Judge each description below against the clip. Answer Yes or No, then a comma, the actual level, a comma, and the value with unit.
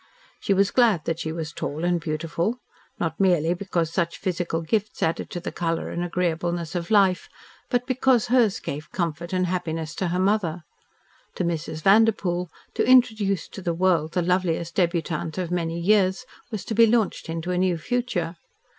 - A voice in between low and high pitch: Yes, medium, 175 Hz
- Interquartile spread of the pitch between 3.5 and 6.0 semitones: No, average, 3.1 semitones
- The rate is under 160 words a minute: No, average, 175 wpm